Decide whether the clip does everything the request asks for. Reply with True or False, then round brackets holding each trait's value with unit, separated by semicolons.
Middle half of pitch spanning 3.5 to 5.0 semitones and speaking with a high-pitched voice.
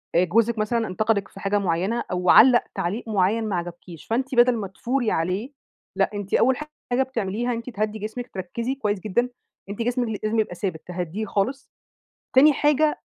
True (4.0 semitones; 215 Hz)